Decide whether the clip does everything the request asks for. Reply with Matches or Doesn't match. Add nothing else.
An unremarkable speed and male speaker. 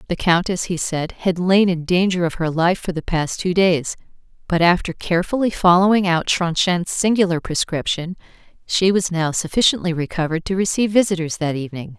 Doesn't match